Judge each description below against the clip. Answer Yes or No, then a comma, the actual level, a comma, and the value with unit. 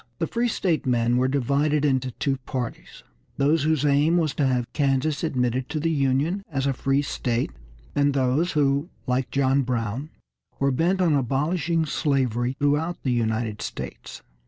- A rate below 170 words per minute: Yes, average, 160 wpm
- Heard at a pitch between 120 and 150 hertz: Yes, medium, 140 Hz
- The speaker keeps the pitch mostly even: No, average, 3.1 semitones